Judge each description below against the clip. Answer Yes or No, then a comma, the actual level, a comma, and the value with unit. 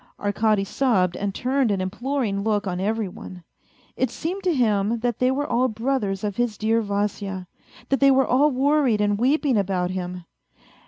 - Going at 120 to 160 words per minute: No, average, 175 wpm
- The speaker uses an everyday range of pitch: Yes, average, 4.8 semitones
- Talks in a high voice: Yes, high, 220 Hz